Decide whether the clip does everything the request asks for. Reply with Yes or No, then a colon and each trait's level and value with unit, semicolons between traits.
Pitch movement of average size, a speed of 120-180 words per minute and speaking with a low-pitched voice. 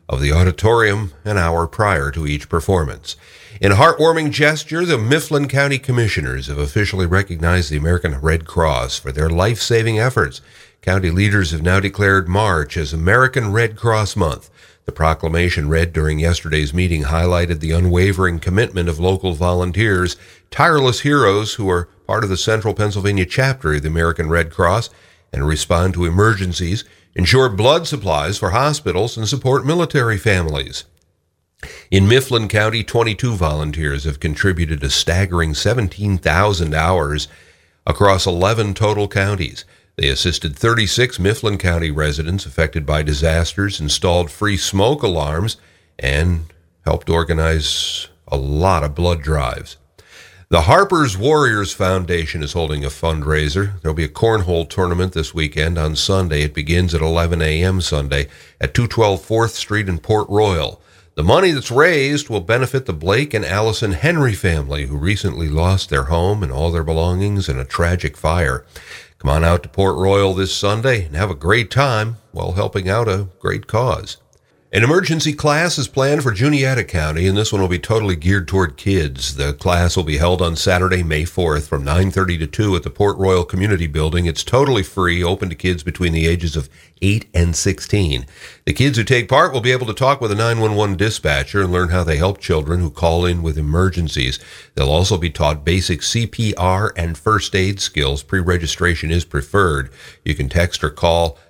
Yes: average, 4.3 semitones; average, 165 wpm; very low, 90 Hz